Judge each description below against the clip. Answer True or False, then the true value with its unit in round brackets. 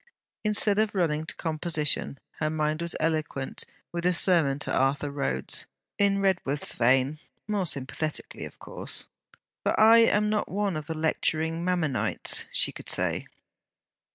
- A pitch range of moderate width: True (4.3 semitones)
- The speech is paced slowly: False (145 wpm)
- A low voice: False (160 Hz)